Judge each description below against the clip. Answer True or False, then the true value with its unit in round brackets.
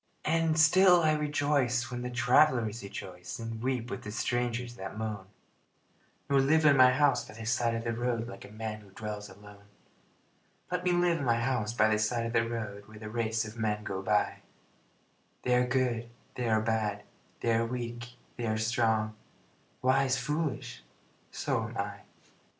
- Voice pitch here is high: False (115 Hz)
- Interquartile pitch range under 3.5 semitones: True (3.0 semitones)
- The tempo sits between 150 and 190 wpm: True (180 wpm)